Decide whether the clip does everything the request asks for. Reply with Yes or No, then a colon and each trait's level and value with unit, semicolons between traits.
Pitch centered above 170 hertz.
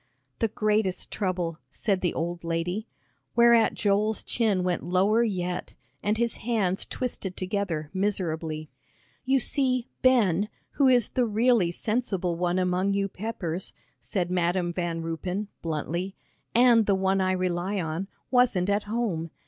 Yes: high, 190 Hz